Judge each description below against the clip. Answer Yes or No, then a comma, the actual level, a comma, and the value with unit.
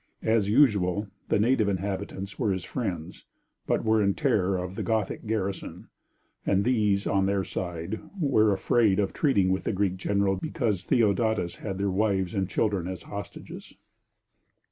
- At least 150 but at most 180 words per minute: Yes, average, 155 wpm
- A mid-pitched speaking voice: No, low, 100 Hz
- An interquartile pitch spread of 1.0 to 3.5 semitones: Yes, narrow, 2.5 semitones